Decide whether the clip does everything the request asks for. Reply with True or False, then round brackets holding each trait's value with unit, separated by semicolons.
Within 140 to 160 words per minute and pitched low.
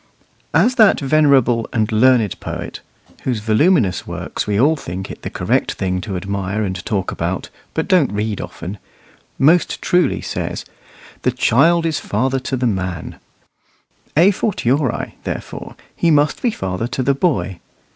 True (150 wpm; 120 Hz)